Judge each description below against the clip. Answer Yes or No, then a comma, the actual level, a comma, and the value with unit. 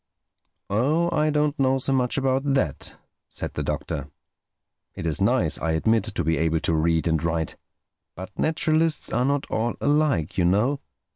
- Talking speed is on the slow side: No, average, 165 wpm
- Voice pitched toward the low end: Yes, low, 120 Hz